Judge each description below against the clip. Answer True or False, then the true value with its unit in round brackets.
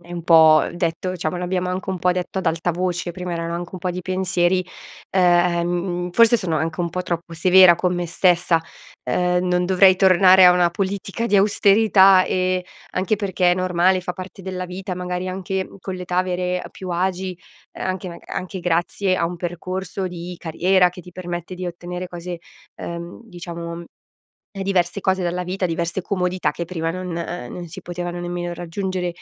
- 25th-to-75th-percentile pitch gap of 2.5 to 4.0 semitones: False (1.2 semitones)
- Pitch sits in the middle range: True (180 Hz)